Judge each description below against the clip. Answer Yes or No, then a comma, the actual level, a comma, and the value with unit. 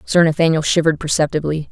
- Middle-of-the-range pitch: Yes, medium, 160 Hz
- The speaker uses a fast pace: No, average, 140 wpm